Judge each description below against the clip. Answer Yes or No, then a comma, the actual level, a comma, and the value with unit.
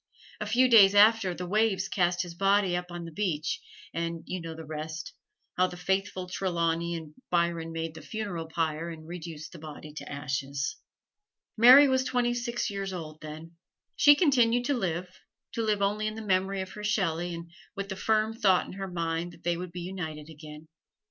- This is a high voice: No, medium, 180 Hz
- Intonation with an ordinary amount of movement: Yes, average, 3.9 semitones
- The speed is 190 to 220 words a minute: Yes, average, 195 wpm